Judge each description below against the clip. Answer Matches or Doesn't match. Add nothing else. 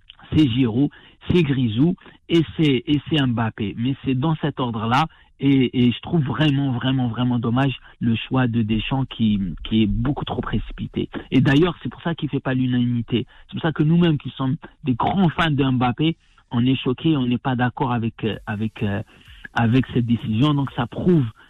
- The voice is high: Doesn't match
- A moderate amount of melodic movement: Matches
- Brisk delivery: Doesn't match